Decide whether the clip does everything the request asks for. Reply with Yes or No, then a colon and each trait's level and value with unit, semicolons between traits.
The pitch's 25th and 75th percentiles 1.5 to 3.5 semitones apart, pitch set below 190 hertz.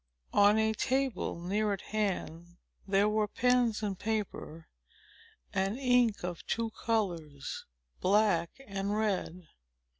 No: average, 3.2 semitones; high, 205 Hz